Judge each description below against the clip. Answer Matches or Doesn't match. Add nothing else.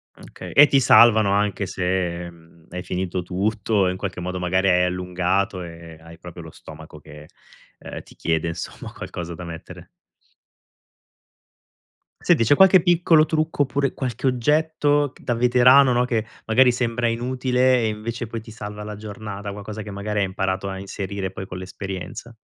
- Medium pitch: Doesn't match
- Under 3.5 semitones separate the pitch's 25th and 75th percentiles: Doesn't match